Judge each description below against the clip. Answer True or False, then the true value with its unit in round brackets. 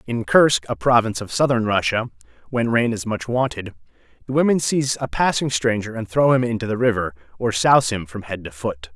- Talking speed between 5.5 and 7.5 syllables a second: True (5.7 syllables/s)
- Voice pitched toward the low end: True (115 Hz)